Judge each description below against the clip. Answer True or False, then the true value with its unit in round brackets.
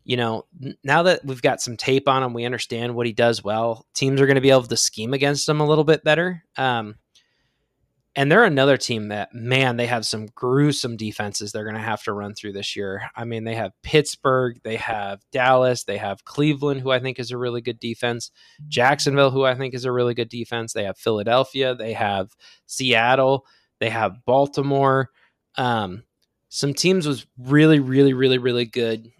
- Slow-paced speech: False (200 wpm)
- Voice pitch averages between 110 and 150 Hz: True (125 Hz)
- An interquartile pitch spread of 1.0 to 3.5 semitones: True (3.1 semitones)